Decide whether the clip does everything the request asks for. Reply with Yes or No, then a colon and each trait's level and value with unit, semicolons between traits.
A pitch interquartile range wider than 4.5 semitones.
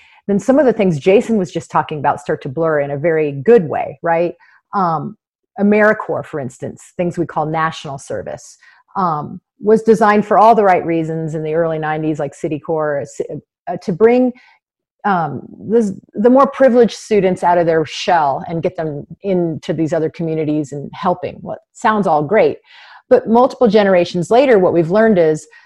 Yes: wide, 5.6 semitones